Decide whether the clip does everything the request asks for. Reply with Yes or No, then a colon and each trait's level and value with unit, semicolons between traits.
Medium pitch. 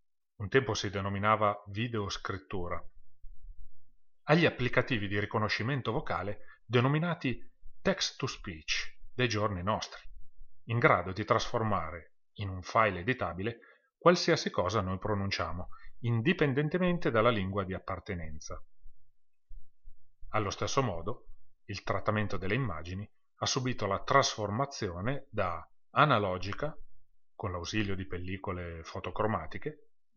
No: low, 110 Hz